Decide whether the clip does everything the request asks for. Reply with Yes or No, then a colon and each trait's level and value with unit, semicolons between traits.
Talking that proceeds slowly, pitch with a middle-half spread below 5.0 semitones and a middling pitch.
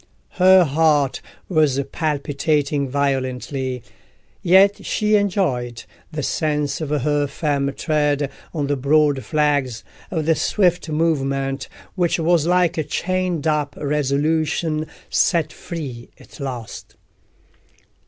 Yes: slow, 105 wpm; average, 2.9 semitones; medium, 150 Hz